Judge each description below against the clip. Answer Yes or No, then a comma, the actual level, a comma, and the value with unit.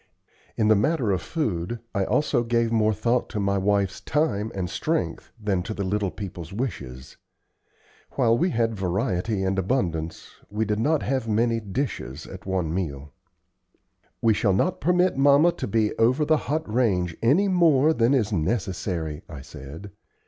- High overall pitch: No, low, 105 Hz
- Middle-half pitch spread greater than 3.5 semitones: Yes, average, 5.1 semitones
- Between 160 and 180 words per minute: Yes, average, 165 wpm